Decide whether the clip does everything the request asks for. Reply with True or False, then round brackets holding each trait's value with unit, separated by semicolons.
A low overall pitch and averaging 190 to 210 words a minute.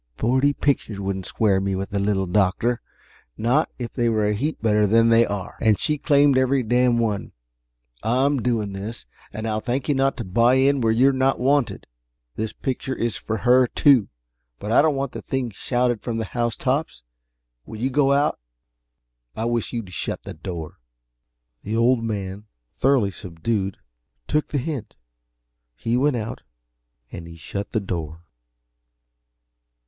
False (115 Hz; 165 wpm)